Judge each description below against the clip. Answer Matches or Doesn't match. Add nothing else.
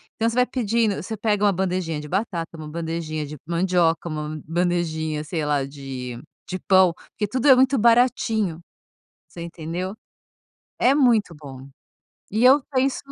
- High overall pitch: Doesn't match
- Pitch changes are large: Matches